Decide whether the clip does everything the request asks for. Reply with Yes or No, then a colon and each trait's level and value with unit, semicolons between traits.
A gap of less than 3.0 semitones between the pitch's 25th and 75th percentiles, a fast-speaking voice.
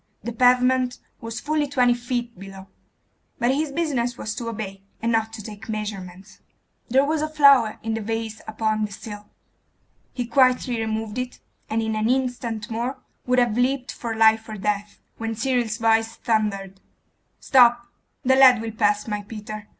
No: narrow, 2.6 semitones; average, 165 wpm